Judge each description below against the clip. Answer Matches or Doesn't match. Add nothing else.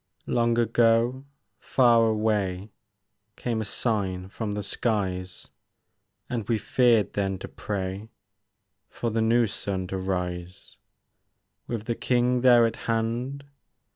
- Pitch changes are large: Doesn't match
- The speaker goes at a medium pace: Doesn't match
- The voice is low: Matches